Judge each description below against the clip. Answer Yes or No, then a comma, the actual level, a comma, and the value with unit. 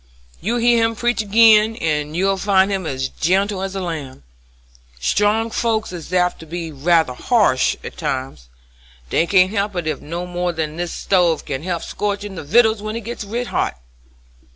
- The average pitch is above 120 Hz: Yes, medium, 185 Hz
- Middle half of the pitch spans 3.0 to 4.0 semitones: No, average, 4.7 semitones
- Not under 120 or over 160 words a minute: No, average, 175 wpm